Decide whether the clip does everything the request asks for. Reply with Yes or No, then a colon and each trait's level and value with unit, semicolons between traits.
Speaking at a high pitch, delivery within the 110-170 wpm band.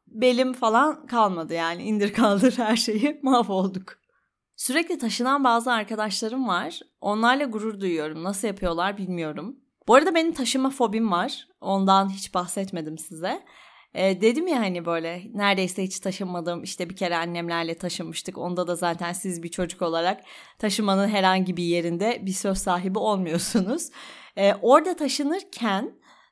Yes: high, 200 Hz; fast, 140 wpm